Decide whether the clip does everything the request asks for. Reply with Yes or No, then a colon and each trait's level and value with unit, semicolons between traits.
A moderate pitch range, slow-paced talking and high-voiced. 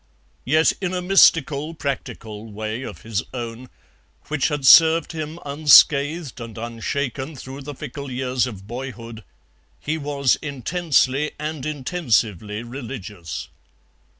No: average, 4.6 semitones; slow, 120 wpm; low, 135 Hz